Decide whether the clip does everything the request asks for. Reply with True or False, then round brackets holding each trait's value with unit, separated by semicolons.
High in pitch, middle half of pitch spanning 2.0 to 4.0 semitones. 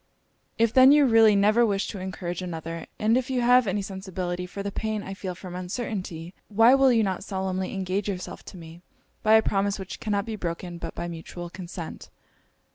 True (195 Hz; 3.4 semitones)